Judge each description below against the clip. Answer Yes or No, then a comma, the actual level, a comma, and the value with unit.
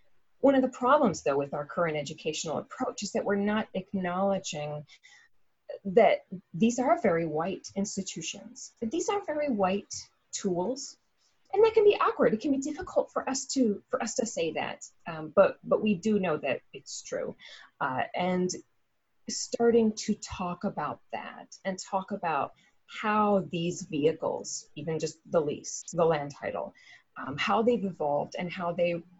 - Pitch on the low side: No, high, 195 Hz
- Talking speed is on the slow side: No, average, 165 wpm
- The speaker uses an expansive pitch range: Yes, wide, 6.7 semitones